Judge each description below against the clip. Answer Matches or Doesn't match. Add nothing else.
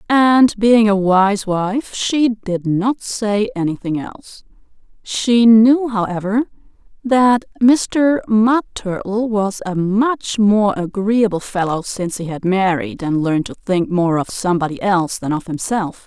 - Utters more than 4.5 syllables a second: Doesn't match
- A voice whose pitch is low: Doesn't match